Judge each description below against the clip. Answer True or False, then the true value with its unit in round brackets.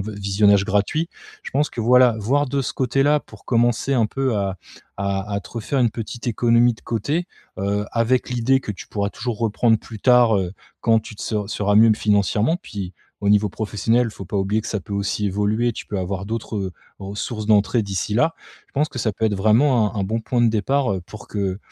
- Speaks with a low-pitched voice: True (110 Hz)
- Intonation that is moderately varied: True (3.2 semitones)